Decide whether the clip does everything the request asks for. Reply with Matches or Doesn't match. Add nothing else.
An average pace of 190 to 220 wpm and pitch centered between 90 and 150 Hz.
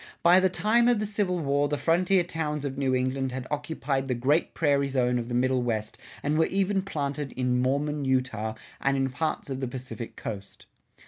Matches